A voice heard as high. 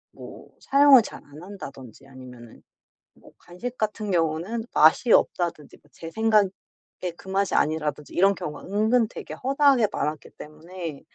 No: medium, 180 Hz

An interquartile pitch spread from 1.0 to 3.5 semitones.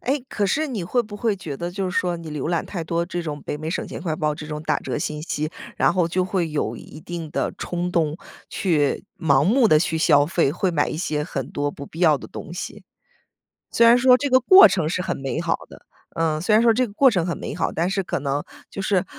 No: average, 4.2 semitones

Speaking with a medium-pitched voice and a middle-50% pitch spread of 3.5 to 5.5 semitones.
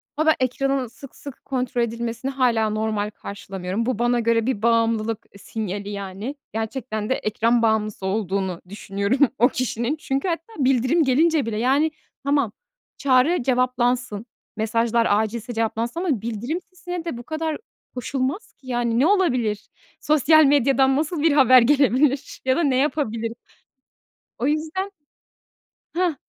No: high, 245 Hz; average, 4.3 semitones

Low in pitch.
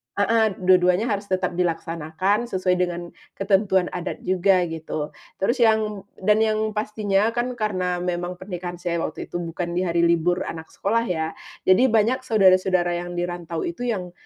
No: medium, 185 Hz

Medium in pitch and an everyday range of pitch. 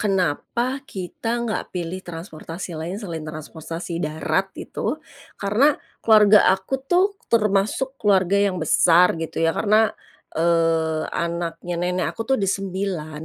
Yes: medium, 180 Hz; average, 3.4 semitones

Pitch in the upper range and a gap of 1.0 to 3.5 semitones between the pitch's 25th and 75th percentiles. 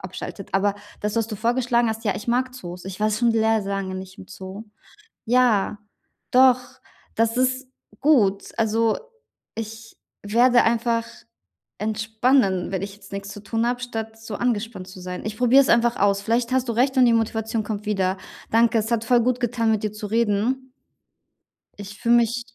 Yes: high, 225 Hz; average, 2.8 semitones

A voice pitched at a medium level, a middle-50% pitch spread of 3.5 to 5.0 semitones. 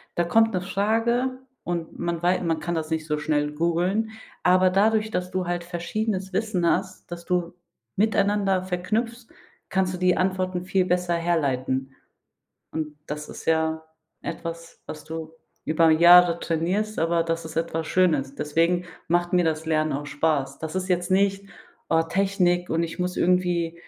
No: medium, 175 Hz; narrow, 2.5 semitones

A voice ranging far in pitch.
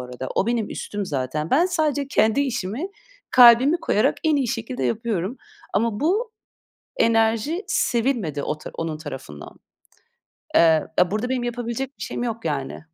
Yes: wide, 7.6 semitones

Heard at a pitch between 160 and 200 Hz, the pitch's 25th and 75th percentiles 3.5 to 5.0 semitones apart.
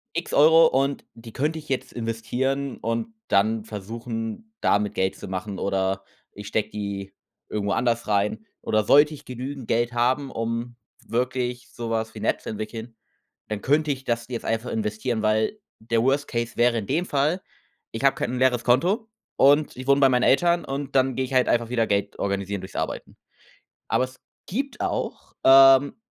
No: low, 120 Hz; average, 3.8 semitones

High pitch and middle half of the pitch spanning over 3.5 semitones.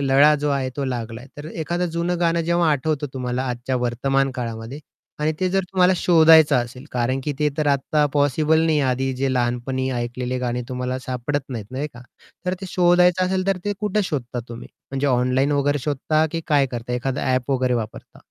No: low, 135 Hz; average, 3.9 semitones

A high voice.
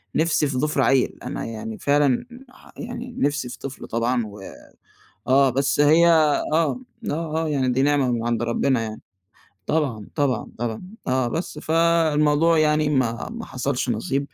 No: medium, 140 Hz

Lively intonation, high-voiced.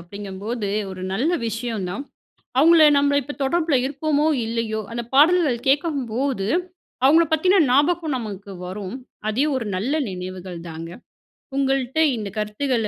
Yes: wide, 5.9 semitones; high, 245 Hz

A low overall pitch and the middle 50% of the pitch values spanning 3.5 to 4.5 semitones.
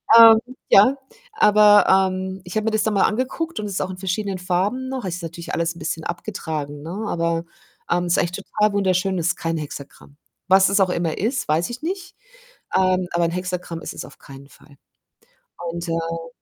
No: medium, 185 Hz; average, 3.8 semitones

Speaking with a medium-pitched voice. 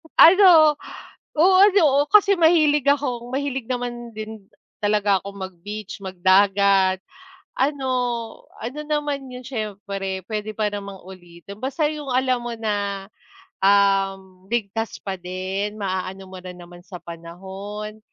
No: high, 210 Hz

